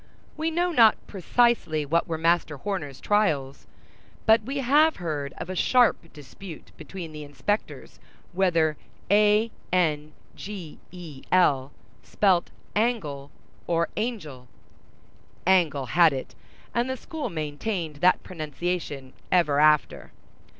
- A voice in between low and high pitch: Yes, medium, 170 Hz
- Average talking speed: No, slow, 120 wpm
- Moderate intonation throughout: No, wide, 5.8 semitones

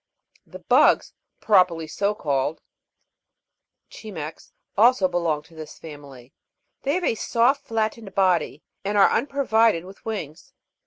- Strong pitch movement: Yes, wide, 5.8 semitones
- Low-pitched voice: No, high, 190 Hz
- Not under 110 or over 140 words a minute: Yes, slow, 135 wpm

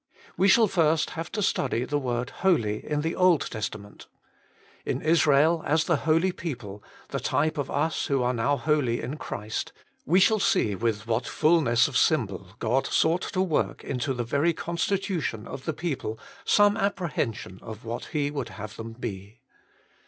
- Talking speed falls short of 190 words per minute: Yes, average, 170 wpm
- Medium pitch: Yes, medium, 145 Hz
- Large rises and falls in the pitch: Yes, wide, 6.2 semitones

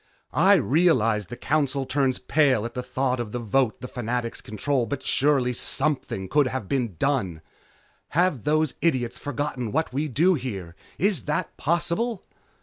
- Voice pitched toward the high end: No, low, 130 Hz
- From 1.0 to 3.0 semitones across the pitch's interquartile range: No, average, 4.2 semitones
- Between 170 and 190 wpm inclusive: No, average, 155 wpm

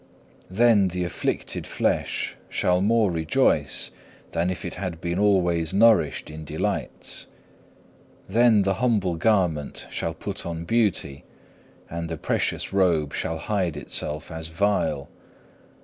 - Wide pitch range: No, average, 3.8 semitones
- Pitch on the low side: Yes, very low, 90 Hz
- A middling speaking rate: No, slow, 125 wpm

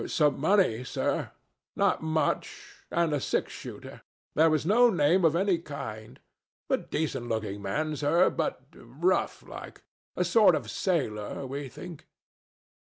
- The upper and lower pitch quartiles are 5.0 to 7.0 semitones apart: Yes, average, 5.3 semitones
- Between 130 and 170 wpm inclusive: Yes, slow, 135 wpm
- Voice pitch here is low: No, medium, 155 Hz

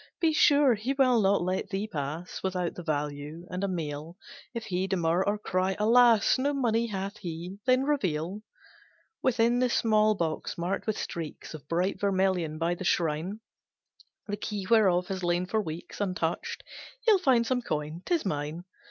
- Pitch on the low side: No, high, 190 Hz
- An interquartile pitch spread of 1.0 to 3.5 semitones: No, average, 4.9 semitones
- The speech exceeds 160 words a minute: Yes, average, 170 wpm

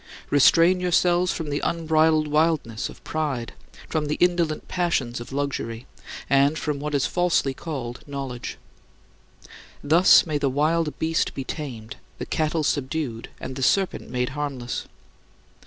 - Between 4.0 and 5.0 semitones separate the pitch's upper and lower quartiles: No, average, 3.5 semitones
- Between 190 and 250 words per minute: No, average, 140 wpm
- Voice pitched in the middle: Yes, medium, 150 Hz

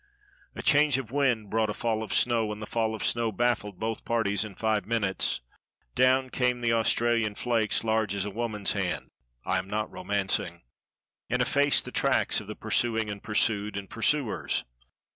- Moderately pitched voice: No, low, 110 Hz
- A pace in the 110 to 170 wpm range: No, average, 180 wpm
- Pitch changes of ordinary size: No, narrow, 2.3 semitones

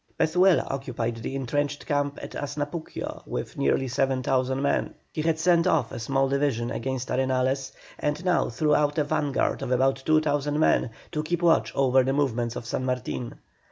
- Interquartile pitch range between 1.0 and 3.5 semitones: Yes, narrow, 2.6 semitones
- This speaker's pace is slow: No, average, 170 wpm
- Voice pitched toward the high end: No, low, 135 Hz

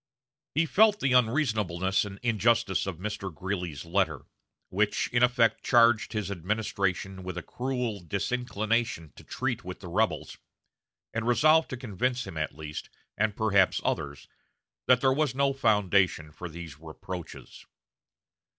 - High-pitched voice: No, low, 105 Hz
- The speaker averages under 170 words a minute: Yes, average, 140 wpm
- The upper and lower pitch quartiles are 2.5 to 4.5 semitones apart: No, average, 5.2 semitones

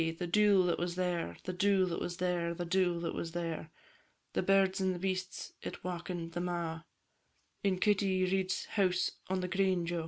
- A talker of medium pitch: Yes, medium, 180 Hz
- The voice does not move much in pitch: Yes, narrow, 1.6 semitones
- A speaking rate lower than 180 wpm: No, average, 185 wpm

